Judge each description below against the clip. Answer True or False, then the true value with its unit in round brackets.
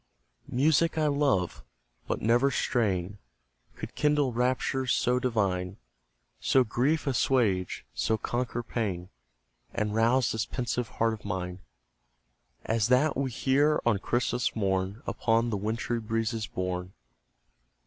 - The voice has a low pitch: True (115 Hz)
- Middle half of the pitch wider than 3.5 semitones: True (4.0 semitones)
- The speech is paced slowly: True (120 wpm)